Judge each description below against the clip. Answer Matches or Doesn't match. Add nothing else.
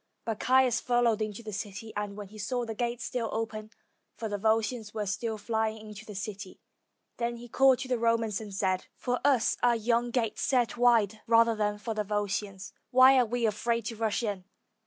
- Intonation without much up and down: Matches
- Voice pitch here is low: Doesn't match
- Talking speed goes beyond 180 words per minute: Matches